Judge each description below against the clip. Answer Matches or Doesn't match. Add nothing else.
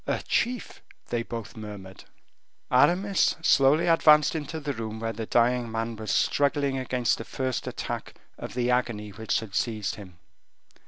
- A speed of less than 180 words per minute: Matches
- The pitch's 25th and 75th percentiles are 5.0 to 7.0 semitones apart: Doesn't match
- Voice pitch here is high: Doesn't match